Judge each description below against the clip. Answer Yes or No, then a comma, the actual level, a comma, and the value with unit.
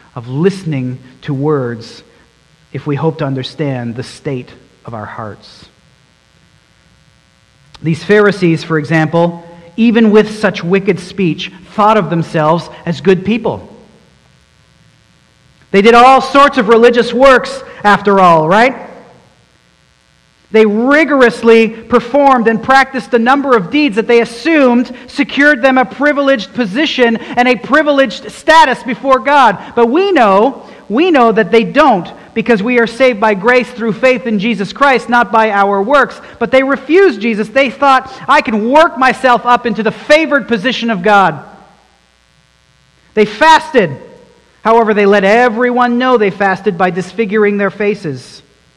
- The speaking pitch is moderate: No, high, 225 Hz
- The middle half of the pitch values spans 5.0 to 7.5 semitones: Yes, wide, 5.5 semitones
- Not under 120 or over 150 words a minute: Yes, average, 140 wpm